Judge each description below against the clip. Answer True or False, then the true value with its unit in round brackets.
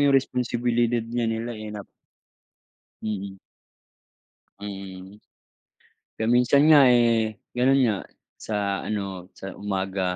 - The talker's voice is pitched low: True (110 Hz)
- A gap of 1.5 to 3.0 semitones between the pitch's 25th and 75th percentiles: False (3.6 semitones)